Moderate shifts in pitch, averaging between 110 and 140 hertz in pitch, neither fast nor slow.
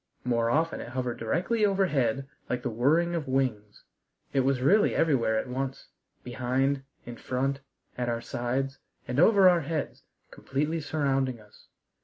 Yes: average, 4.0 semitones; low, 135 Hz; average, 150 wpm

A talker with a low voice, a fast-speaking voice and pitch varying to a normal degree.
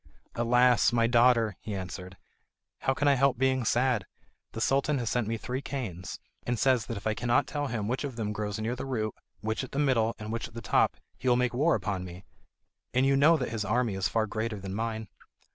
Yes: low, 115 Hz; fast, 230 wpm; average, 3.1 semitones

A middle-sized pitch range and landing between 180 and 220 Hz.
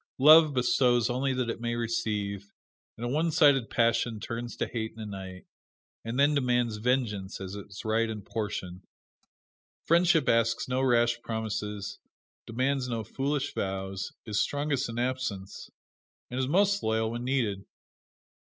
No: average, 3.6 semitones; low, 120 Hz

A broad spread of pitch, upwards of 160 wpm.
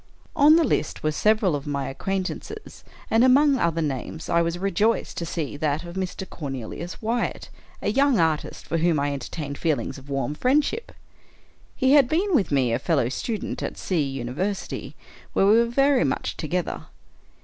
Yes: wide, 8.6 semitones; average, 170 wpm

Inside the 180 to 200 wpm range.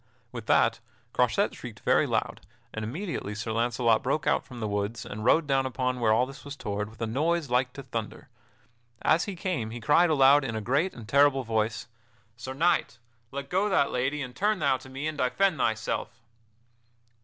Yes: average, 195 wpm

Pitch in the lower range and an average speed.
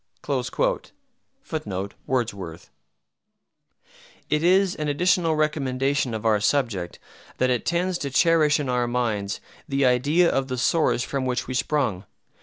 No: low, 130 Hz; slow, 130 wpm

